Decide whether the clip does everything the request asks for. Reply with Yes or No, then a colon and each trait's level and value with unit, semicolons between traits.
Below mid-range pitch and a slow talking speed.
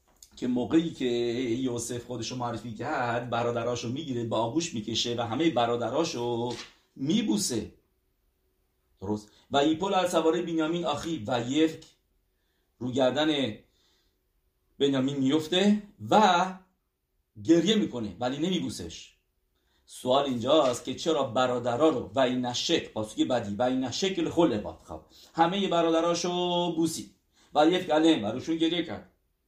Yes: low, 125 Hz; slow, 120 wpm